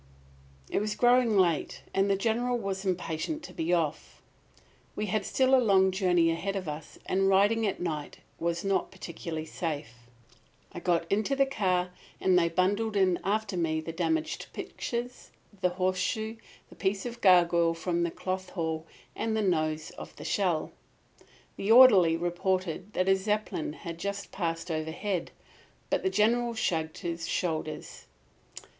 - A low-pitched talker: No, medium, 185 Hz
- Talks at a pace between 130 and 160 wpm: Yes, average, 155 wpm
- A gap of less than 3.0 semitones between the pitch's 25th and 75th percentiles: No, average, 3.9 semitones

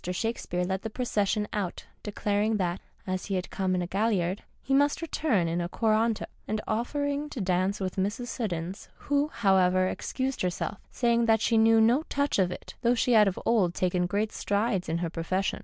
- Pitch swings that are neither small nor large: Yes, average, 4.0 semitones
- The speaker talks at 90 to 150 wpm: No, average, 195 wpm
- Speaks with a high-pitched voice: Yes, high, 205 Hz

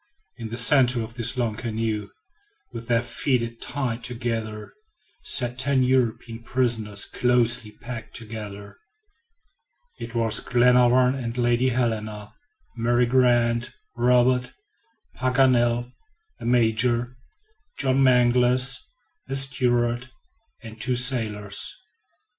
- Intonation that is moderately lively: No, narrow, 1.7 semitones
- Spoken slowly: Yes, slow, 105 wpm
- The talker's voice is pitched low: Yes, low, 120 Hz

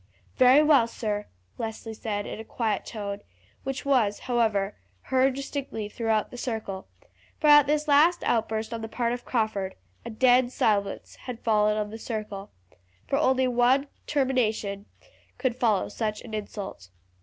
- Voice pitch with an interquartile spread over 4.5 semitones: No, average, 3.4 semitones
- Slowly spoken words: No, average, 155 wpm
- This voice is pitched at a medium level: No, high, 225 Hz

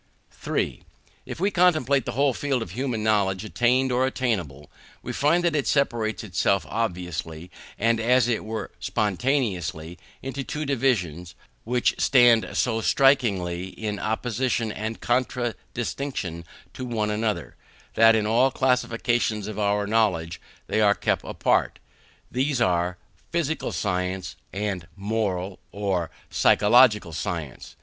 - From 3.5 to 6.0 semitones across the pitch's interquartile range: Yes, average, 5.0 semitones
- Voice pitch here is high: No, low, 110 Hz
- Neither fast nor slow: No, slow, 130 wpm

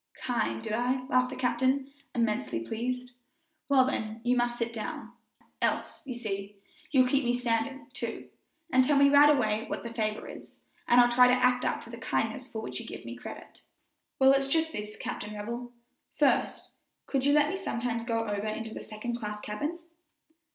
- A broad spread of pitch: No, average, 2.8 semitones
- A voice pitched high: Yes, high, 240 Hz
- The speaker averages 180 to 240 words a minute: Yes, average, 190 wpm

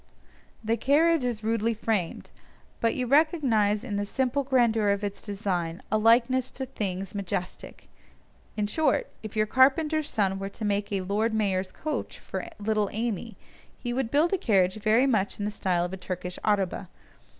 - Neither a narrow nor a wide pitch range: Yes, average, 4.1 semitones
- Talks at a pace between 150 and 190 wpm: Yes, average, 170 wpm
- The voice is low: No, high, 215 Hz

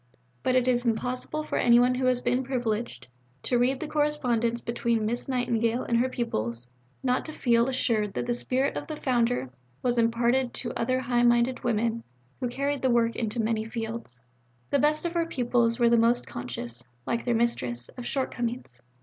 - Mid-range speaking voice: No, high, 240 Hz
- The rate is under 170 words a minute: No, average, 185 wpm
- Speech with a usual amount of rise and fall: No, narrow, 1.7 semitones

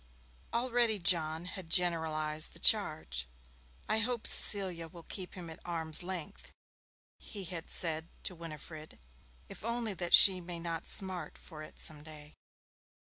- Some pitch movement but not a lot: Yes, average, 3.2 semitones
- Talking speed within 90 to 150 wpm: Yes, average, 140 wpm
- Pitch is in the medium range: Yes, medium, 170 Hz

